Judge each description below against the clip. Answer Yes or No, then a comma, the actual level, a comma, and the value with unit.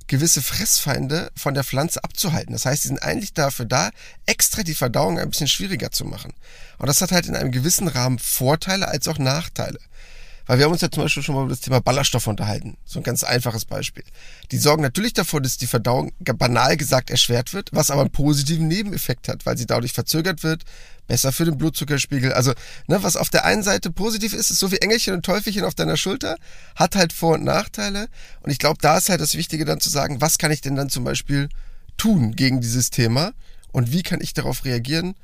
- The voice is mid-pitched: Yes, medium, 145 Hz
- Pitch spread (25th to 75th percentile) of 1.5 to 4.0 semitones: No, average, 4.6 semitones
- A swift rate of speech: Yes, fast, 220 wpm